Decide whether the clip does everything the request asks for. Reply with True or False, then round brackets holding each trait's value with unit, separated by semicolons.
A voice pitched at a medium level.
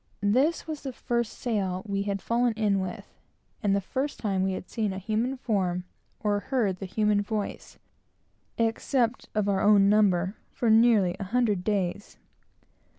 False (210 Hz)